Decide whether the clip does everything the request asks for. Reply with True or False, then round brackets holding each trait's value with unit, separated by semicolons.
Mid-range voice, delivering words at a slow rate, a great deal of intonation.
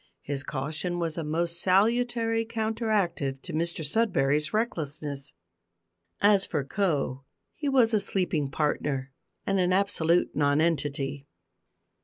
True (170 Hz; 115 wpm; 6.0 semitones)